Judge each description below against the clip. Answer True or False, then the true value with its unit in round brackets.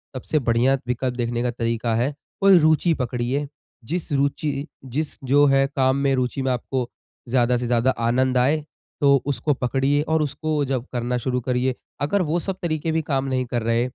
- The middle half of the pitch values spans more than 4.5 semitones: False (2.8 semitones)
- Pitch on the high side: False (130 Hz)